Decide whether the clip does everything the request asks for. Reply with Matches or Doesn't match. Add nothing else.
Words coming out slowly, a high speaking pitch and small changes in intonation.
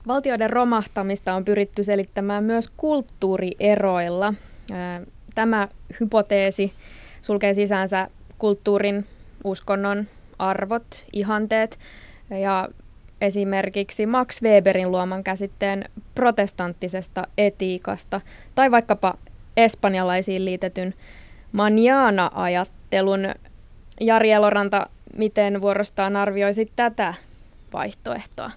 Matches